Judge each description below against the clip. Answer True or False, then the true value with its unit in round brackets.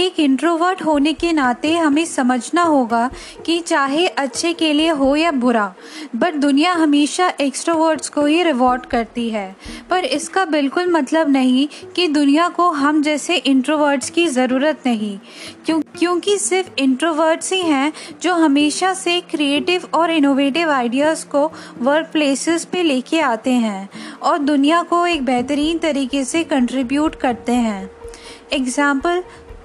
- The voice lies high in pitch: True (300 Hz)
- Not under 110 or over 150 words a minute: True (140 wpm)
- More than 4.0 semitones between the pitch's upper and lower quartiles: False (3.7 semitones)